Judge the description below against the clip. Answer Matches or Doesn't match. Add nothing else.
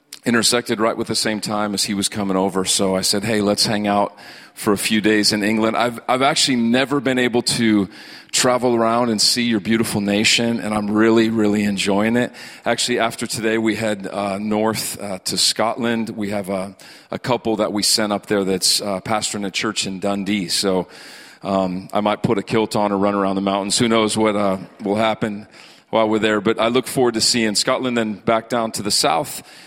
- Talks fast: Matches